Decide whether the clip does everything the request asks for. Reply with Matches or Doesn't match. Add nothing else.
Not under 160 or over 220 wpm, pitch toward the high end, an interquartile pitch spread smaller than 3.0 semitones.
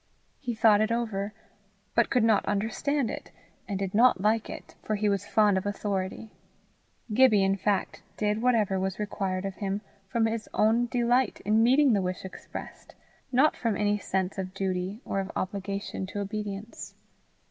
Matches